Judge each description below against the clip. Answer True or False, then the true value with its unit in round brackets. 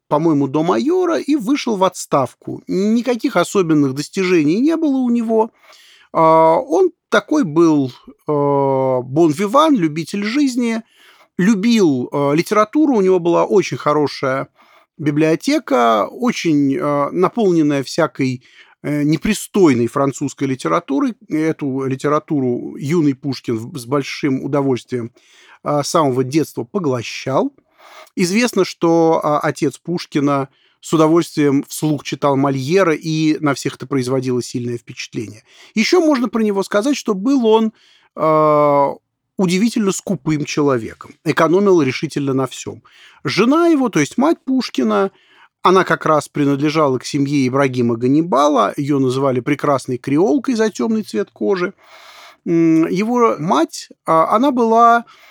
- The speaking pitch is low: False (160 Hz)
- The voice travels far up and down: True (7.8 semitones)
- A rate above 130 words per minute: False (115 wpm)